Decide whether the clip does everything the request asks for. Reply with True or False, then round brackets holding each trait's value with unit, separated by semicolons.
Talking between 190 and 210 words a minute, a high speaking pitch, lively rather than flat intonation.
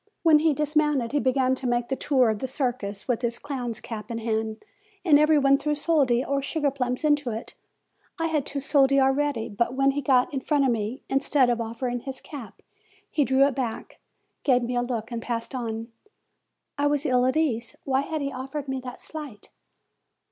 False (205 wpm; 265 Hz; 3.2 semitones)